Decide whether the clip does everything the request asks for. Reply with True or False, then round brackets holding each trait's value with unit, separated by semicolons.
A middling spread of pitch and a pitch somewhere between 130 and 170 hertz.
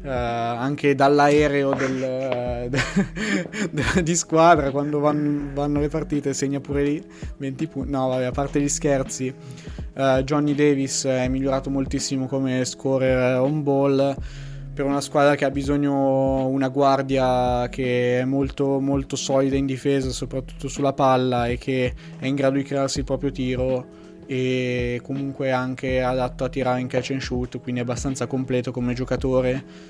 False (1.7 semitones; 135 Hz)